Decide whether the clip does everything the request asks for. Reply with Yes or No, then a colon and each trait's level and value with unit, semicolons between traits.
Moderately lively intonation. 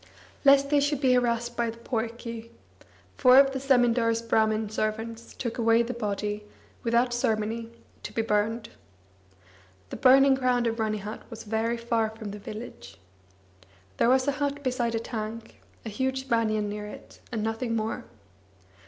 No: narrow, 2.3 semitones